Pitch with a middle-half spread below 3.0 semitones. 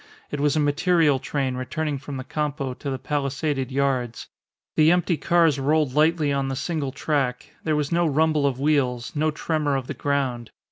Yes: narrow, 2.5 semitones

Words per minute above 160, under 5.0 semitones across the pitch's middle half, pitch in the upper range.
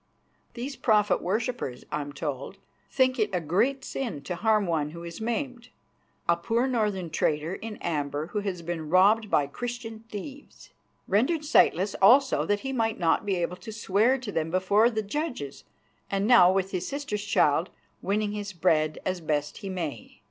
No: average, 175 wpm; average, 5.3 semitones; high, 200 Hz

